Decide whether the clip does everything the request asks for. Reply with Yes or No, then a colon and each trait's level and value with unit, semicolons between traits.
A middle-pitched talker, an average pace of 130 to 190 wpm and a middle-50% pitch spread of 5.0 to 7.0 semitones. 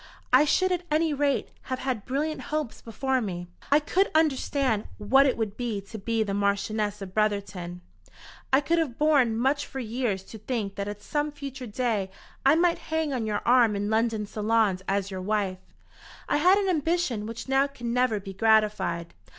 No: high, 230 Hz; average, 185 wpm; wide, 5.4 semitones